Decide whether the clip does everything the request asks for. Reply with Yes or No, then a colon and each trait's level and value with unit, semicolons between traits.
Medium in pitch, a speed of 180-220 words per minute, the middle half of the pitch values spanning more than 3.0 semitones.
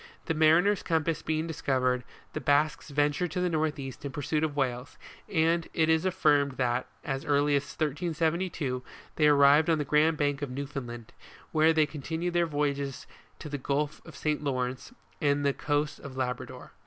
No: medium, 145 Hz; average, 185 wpm; narrow, 2.4 semitones